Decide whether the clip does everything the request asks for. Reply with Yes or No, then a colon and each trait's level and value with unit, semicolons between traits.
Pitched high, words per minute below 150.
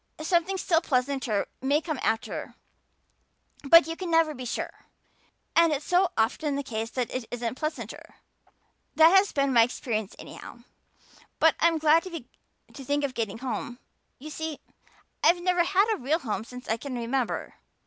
No: very high, 285 Hz; average, 160 wpm